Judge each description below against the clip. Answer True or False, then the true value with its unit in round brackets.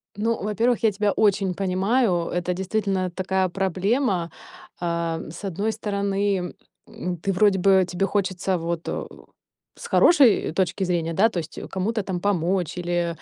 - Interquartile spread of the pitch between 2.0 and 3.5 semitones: True (2.6 semitones)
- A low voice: False (190 Hz)